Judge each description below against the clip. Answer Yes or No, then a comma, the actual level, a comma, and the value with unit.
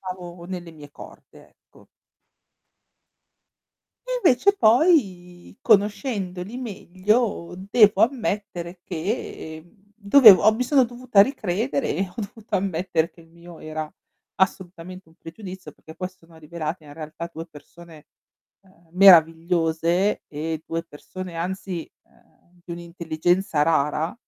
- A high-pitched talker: No, medium, 180 Hz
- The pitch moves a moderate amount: Yes, average, 3.7 semitones